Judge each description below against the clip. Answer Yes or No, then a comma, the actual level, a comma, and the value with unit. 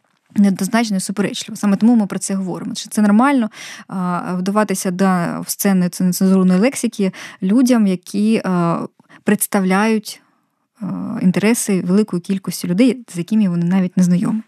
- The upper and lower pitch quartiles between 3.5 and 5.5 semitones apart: No, average, 2.8 semitones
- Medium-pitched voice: No, high, 200 Hz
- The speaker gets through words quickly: No, average, 125 wpm